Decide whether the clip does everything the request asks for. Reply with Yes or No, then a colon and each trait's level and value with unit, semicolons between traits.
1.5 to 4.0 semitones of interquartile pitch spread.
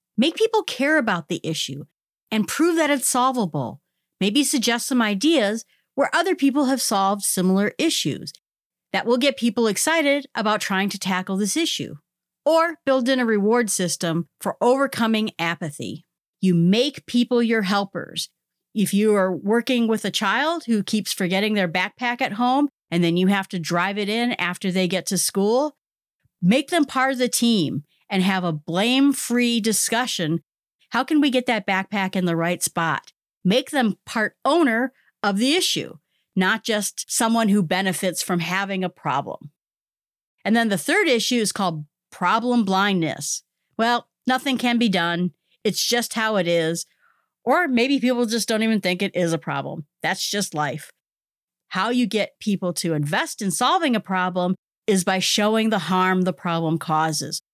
No: average, 5.0 semitones